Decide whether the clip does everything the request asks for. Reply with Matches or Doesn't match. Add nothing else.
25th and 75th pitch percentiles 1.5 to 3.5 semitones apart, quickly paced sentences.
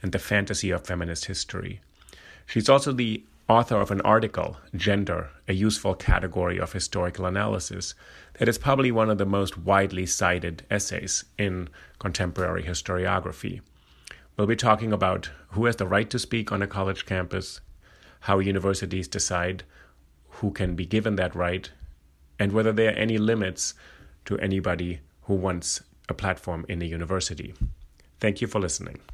Doesn't match